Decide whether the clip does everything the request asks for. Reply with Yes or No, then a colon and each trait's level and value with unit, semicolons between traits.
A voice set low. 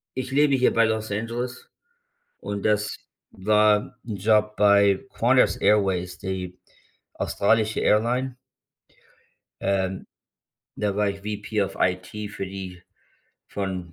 Yes: low, 105 Hz